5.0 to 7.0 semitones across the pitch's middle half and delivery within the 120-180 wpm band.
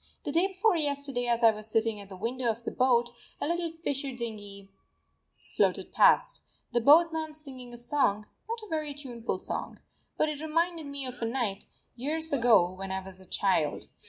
No: wide, 5.5 semitones; average, 190 wpm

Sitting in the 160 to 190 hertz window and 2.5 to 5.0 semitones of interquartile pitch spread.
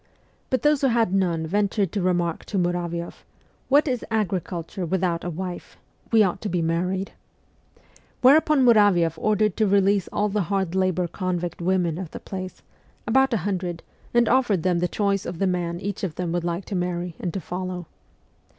Yes: medium, 185 Hz; average, 2.9 semitones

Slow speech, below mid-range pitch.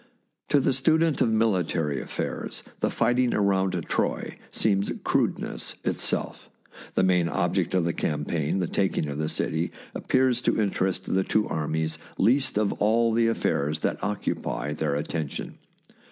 No: average, 155 wpm; very low, 95 Hz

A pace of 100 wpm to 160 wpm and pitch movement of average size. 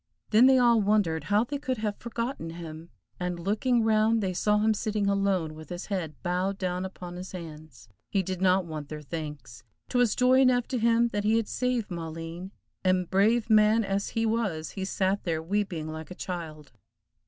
No: average, 190 wpm; average, 4.7 semitones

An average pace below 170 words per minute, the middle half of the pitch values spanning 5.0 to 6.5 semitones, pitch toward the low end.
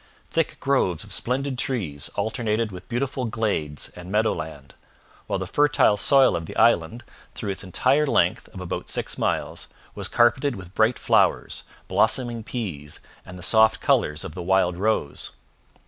Yes: average, 160 wpm; wide, 5.6 semitones; low, 110 Hz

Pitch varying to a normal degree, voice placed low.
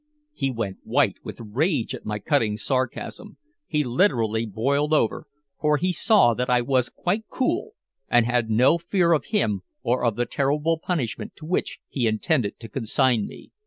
No: wide, 5.7 semitones; low, 130 Hz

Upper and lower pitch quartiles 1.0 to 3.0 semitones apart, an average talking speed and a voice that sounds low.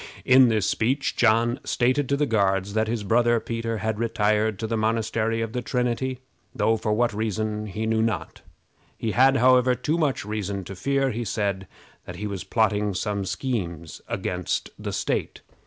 Yes: narrow, 2.6 semitones; average, 175 wpm; low, 110 Hz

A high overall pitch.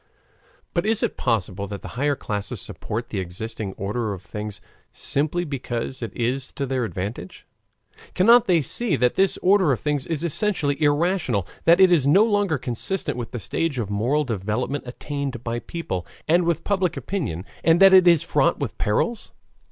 No: medium, 140 Hz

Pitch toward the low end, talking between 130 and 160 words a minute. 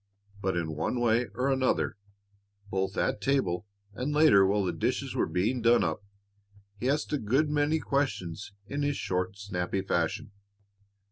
Yes: low, 110 Hz; average, 155 wpm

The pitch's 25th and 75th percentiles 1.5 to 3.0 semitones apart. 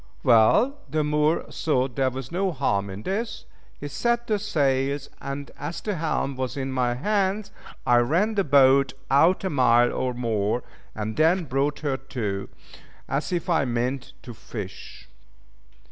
No: average, 5.2 semitones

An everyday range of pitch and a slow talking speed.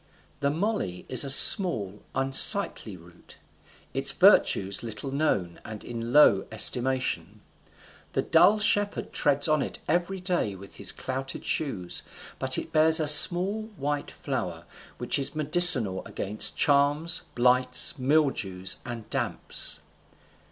No: wide, 6.5 semitones; slow, 130 wpm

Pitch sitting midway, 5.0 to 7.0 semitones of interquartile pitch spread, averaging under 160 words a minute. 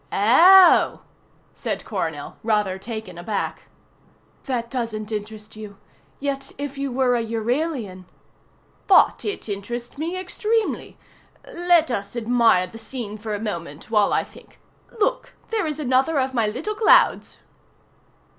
No: high, 235 Hz; average, 5.3 semitones; slow, 135 wpm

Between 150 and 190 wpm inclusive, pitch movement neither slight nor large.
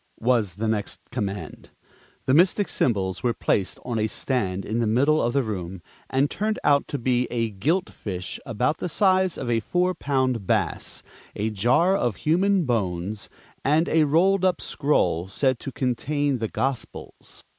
No: average, 165 wpm; wide, 6.2 semitones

